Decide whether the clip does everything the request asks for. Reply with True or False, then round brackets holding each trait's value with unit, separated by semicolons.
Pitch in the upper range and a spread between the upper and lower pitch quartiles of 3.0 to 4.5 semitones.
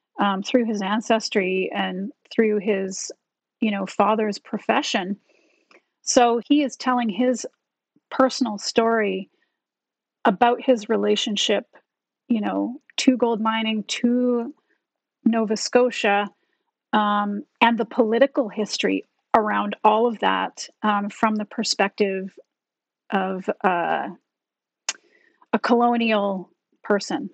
True (225 Hz; 3.3 semitones)